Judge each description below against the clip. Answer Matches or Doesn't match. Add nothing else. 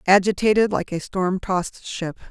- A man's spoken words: Doesn't match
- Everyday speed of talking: Matches